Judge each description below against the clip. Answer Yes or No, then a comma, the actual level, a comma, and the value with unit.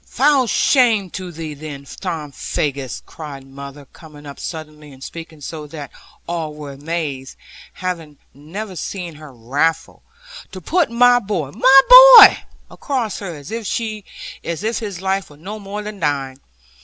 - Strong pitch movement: Yes, wide, 6.2 semitones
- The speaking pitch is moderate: Yes, medium, 165 Hz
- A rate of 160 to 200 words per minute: No, average, 145 wpm